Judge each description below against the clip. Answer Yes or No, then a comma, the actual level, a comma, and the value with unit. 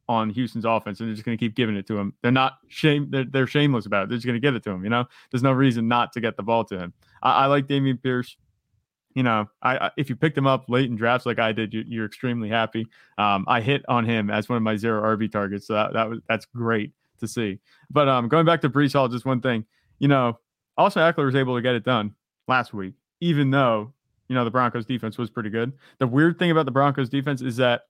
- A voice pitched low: Yes, low, 120 Hz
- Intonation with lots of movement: No, average, 3.3 semitones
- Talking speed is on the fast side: Yes, fast, 270 wpm